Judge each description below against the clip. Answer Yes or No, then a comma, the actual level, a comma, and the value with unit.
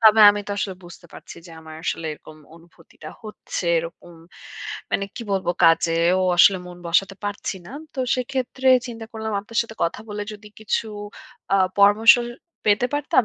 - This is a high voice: Yes, high, 205 Hz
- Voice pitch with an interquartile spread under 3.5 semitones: No, average, 4.4 semitones